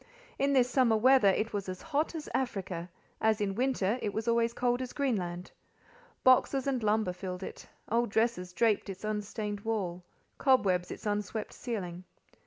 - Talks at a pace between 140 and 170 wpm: Yes, average, 155 wpm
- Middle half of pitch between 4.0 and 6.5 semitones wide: Yes, average, 4.4 semitones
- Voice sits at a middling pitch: No, high, 215 Hz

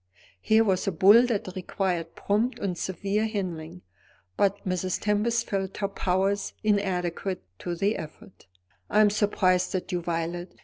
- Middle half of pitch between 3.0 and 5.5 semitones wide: No, narrow, 2.4 semitones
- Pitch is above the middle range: Yes, high, 195 Hz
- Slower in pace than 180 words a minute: Yes, average, 145 wpm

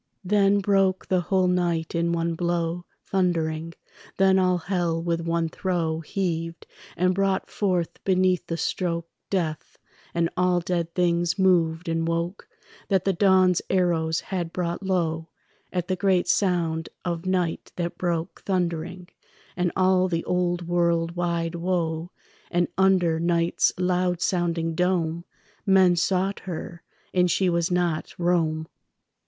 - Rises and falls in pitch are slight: Yes, narrow, 1.7 semitones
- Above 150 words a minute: No, slow, 135 wpm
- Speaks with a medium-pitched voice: Yes, medium, 175 Hz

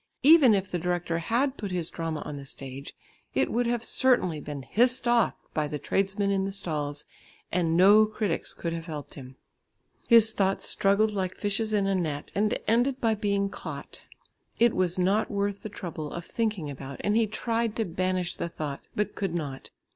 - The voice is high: Yes, high, 195 Hz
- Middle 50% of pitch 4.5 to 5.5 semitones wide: Yes, average, 4.8 semitones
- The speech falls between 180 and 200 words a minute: Yes, average, 190 wpm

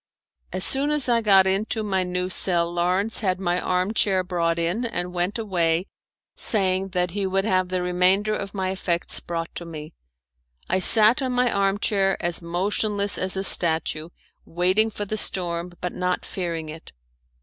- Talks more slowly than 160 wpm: No, average, 175 wpm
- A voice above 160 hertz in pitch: Yes, medium, 185 Hz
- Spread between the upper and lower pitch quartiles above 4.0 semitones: No, narrow, 2.6 semitones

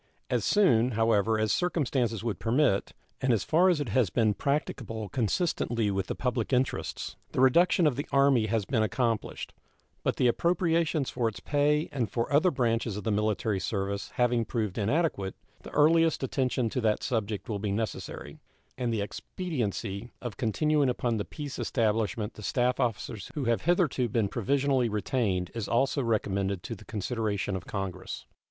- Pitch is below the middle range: Yes, low, 115 Hz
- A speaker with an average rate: Yes, average, 170 wpm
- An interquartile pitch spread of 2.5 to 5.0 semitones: Yes, average, 4.4 semitones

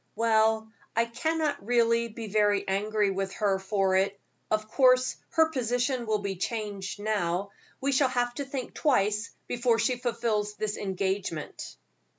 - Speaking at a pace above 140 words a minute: Yes, average, 150 wpm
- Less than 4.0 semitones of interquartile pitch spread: Yes, average, 3.3 semitones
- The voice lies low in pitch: No, high, 220 Hz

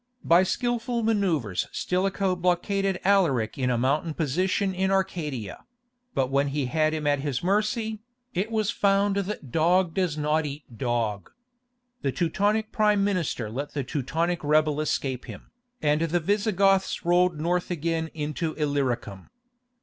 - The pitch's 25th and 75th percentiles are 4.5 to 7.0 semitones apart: Yes, average, 5.3 semitones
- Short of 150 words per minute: Yes, average, 140 wpm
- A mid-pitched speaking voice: Yes, medium, 165 Hz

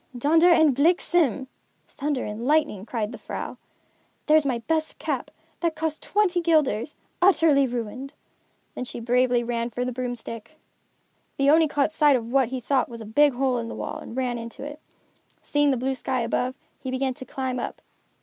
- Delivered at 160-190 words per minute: Yes, average, 180 wpm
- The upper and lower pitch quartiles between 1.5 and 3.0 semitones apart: No, average, 3.8 semitones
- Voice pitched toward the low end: No, very high, 265 Hz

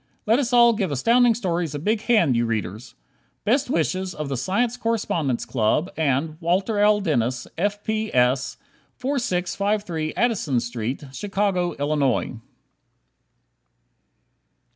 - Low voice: No, medium, 180 Hz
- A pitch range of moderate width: No, wide, 7.9 semitones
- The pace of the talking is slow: Yes, slow, 120 wpm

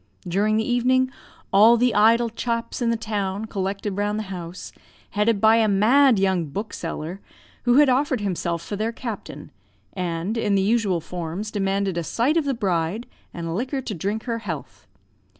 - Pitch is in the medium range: No, high, 210 Hz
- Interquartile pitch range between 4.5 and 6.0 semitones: No, average, 3.5 semitones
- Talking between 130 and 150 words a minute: No, average, 170 wpm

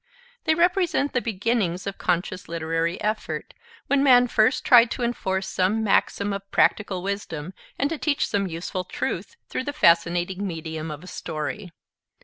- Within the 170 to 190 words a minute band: No, average, 155 wpm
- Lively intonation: Yes, wide, 5.8 semitones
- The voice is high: Yes, high, 195 Hz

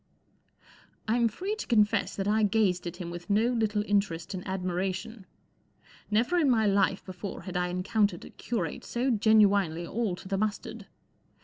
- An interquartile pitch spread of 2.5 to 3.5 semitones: Yes, average, 3.1 semitones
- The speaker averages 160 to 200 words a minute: Yes, average, 170 wpm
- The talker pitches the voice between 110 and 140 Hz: No, high, 205 Hz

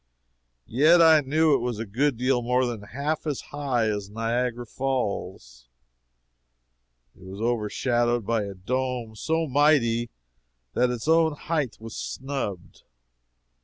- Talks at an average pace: No, slow, 130 wpm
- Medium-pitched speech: No, low, 120 Hz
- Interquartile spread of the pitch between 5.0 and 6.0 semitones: No, average, 4.1 semitones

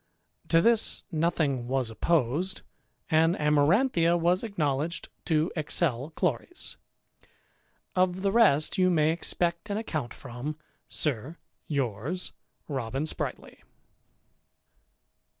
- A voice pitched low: No, medium, 160 Hz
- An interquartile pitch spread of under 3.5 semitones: No, average, 4.4 semitones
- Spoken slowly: Yes, slow, 95 wpm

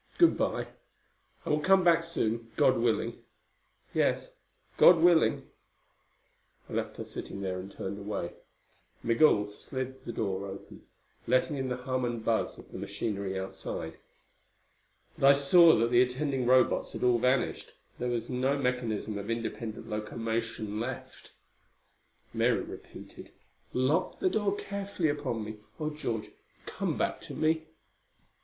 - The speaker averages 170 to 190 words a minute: No, average, 140 wpm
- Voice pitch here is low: Yes, low, 125 Hz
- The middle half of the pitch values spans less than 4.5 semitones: No, average, 5.0 semitones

